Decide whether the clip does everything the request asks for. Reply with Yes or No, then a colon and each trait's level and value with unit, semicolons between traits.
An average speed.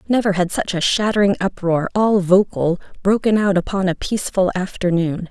Yes: average, 160 wpm